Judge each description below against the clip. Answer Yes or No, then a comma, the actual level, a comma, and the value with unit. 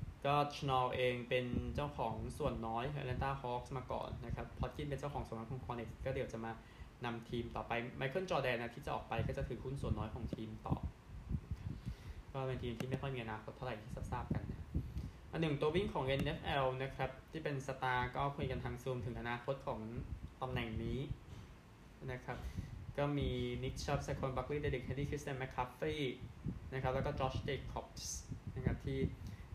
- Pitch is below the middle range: Yes, low, 125 Hz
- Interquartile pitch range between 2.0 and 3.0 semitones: Yes, average, 2.7 semitones